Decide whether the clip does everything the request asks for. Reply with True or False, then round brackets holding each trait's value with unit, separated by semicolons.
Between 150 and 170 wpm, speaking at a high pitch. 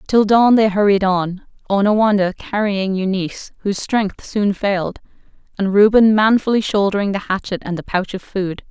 True (160 wpm; 200 Hz)